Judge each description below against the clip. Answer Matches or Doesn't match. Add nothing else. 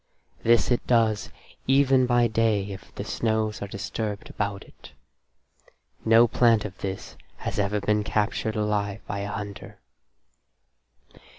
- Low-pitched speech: Matches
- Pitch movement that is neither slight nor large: Doesn't match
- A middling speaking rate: Doesn't match